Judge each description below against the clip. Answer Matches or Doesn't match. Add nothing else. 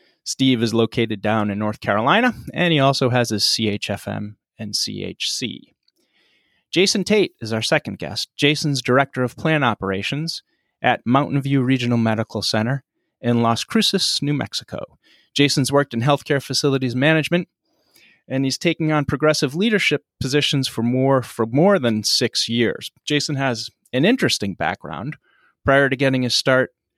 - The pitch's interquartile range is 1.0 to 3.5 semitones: Doesn't match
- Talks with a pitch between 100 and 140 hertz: Matches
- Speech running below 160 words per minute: Matches